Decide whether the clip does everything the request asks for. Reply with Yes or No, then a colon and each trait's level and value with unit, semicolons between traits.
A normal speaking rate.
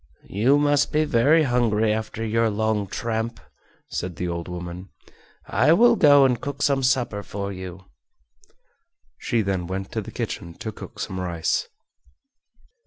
Yes: average, 145 wpm